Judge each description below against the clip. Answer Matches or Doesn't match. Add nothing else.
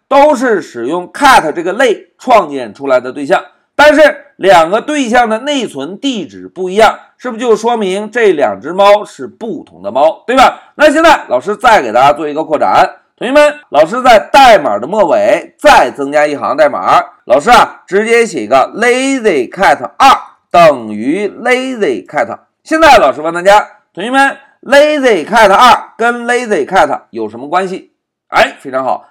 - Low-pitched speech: Doesn't match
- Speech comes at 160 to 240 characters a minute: Doesn't match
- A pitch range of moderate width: Doesn't match